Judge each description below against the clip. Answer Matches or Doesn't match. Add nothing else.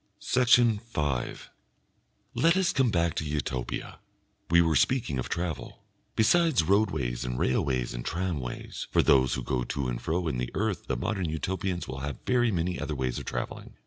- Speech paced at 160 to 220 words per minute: Matches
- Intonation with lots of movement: Matches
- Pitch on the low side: Matches